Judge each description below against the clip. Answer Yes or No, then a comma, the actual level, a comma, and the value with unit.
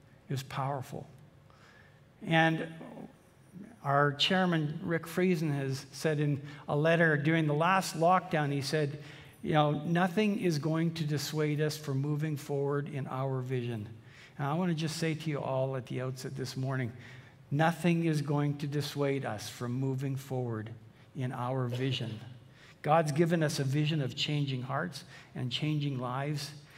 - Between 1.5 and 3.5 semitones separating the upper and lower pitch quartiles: Yes, average, 2.9 semitones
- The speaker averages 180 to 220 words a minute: No, average, 155 wpm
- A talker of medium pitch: Yes, medium, 145 Hz